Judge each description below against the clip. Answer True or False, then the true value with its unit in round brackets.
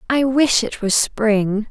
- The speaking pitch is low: False (230 Hz)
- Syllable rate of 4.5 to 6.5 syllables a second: False (4.0 syllables/s)